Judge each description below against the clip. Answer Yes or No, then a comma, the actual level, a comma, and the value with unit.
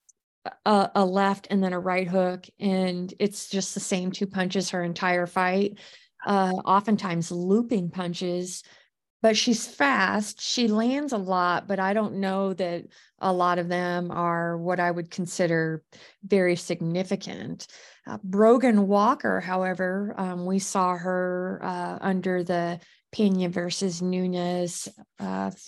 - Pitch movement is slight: Yes, narrow, 1.9 semitones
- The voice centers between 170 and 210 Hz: Yes, medium, 185 Hz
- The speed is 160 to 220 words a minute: No, average, 140 wpm